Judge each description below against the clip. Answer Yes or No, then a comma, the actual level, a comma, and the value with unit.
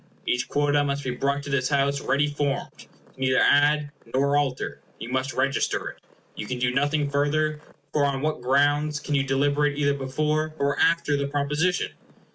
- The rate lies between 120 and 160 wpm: No, average, 185 wpm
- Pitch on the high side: No, medium, 140 Hz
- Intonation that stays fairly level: Yes, narrow, 1.3 semitones